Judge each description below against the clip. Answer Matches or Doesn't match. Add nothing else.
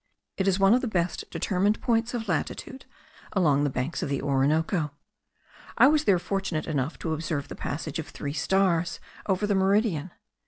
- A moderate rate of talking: Matches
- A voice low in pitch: Doesn't match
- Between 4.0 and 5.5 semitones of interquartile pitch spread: Matches